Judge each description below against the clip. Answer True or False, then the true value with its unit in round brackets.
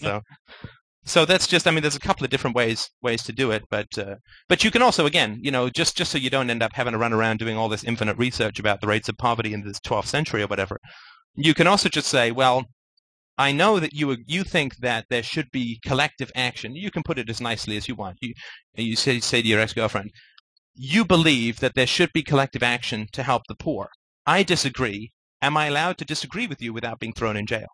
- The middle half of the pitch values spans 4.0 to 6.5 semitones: True (4.9 semitones)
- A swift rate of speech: True (240 wpm)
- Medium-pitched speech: False (125 Hz)